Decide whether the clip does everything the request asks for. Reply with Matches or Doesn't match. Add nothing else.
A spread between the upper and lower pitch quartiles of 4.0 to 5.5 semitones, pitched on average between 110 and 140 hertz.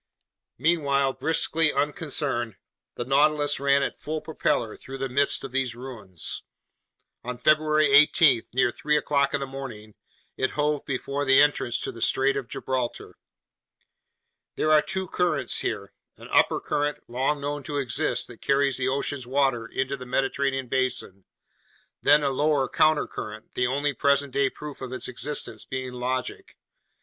Doesn't match